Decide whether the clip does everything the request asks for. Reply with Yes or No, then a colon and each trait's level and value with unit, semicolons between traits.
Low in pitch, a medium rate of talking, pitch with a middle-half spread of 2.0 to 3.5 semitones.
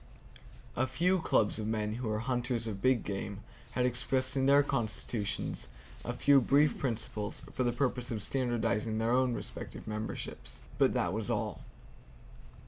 Yes: low, 120 Hz; average, 155 wpm; average, 3.2 semitones